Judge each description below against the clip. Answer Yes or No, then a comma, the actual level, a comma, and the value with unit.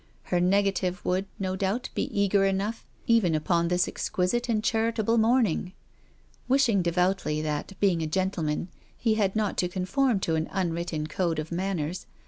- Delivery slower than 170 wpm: Yes, average, 160 wpm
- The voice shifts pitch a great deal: No, average, 3.6 semitones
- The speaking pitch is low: No, high, 190 Hz